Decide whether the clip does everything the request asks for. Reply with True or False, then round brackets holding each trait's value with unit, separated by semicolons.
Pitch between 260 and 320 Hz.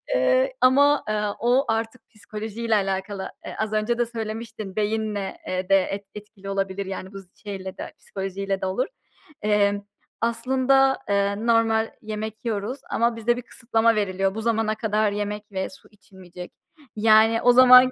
False (215 Hz)